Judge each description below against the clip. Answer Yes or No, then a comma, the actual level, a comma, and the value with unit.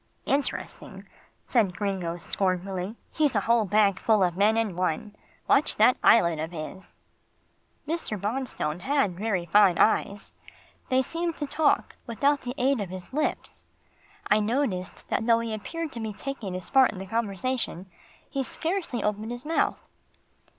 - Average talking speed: Yes, average, 155 wpm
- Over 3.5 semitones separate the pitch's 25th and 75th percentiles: Yes, wide, 5.6 semitones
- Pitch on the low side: No, high, 215 Hz